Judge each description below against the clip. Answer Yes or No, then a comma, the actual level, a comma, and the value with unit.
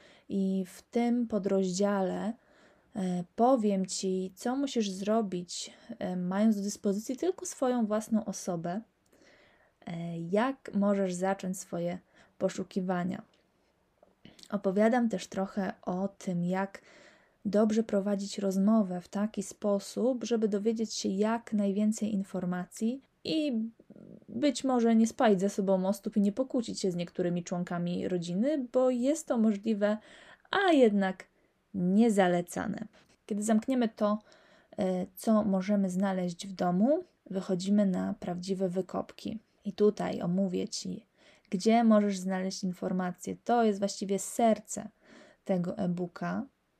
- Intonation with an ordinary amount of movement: Yes, average, 3.1 semitones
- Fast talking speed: No, average, 115 wpm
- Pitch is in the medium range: No, high, 205 Hz